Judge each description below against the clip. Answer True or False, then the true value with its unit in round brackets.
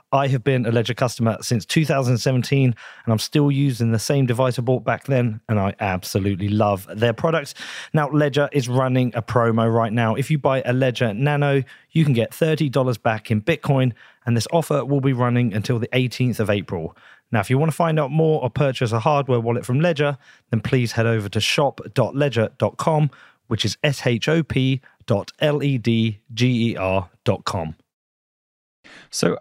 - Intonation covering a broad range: False (3.7 semitones)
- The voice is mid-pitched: False (125 Hz)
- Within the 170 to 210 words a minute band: True (190 wpm)